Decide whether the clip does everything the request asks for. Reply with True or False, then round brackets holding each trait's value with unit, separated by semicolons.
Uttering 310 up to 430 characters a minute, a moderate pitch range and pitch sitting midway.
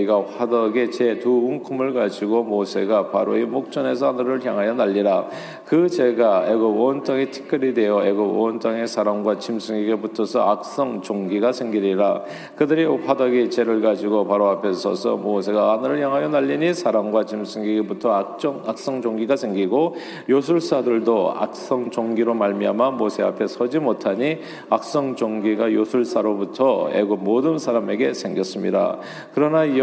False (335 characters per minute; 3.8 semitones; 115 Hz)